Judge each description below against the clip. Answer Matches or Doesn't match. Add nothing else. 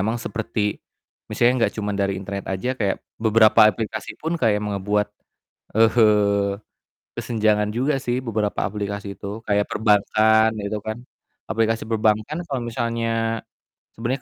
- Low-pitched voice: Matches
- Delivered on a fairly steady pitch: Matches